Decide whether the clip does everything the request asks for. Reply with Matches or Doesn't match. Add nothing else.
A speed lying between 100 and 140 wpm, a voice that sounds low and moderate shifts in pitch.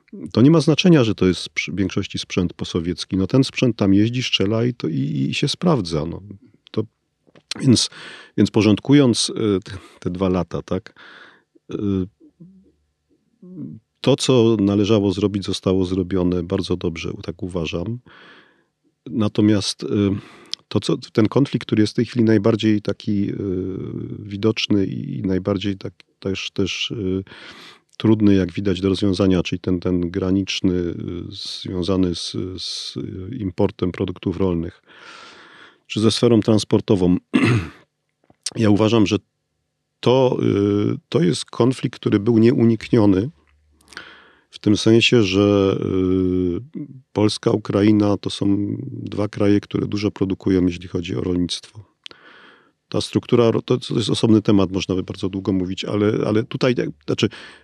Matches